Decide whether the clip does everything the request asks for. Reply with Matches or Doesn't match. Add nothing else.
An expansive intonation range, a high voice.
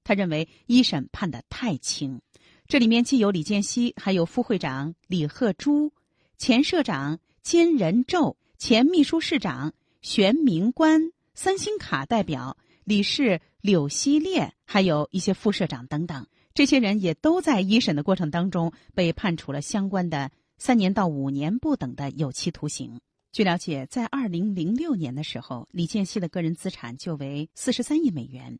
Matches